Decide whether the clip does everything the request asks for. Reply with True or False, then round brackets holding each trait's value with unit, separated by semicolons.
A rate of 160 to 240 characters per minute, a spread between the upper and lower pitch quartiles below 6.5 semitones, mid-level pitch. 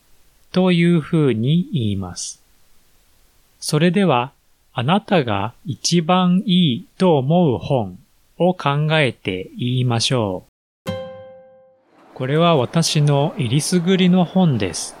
False (200 characters per minute; 8.2 semitones; 150 Hz)